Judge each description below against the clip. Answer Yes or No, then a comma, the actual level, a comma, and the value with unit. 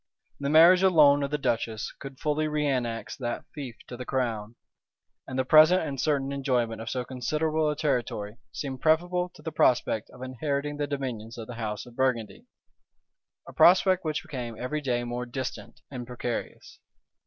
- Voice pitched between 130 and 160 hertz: Yes, low, 135 Hz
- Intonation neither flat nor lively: Yes, average, 3.9 semitones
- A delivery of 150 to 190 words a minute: Yes, average, 170 wpm